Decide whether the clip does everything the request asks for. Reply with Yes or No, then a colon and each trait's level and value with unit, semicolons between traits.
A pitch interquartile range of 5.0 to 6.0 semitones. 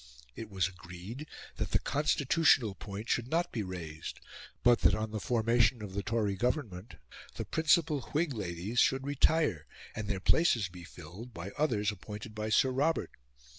Yes: wide, 5.4 semitones